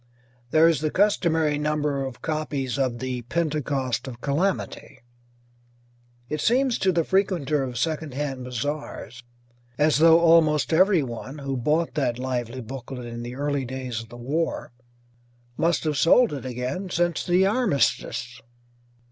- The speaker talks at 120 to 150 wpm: Yes, average, 140 wpm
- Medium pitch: Yes, medium, 145 Hz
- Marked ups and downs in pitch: No, average, 4.3 semitones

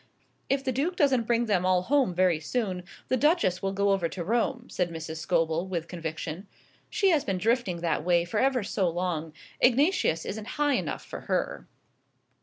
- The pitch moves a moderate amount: No, wide, 6.7 semitones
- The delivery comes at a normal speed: Yes, average, 185 wpm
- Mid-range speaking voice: No, high, 195 Hz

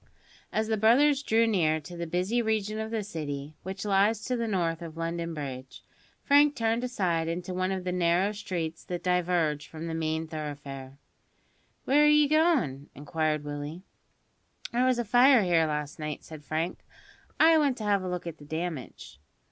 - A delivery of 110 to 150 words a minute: No, average, 180 wpm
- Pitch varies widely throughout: Yes, wide, 5.8 semitones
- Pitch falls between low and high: Yes, medium, 180 Hz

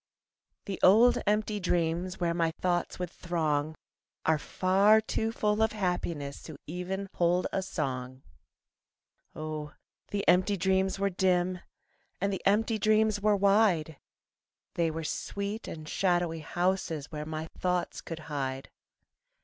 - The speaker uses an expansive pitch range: No, average, 3.9 semitones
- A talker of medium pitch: Yes, medium, 180 Hz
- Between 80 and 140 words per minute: Yes, slow, 135 wpm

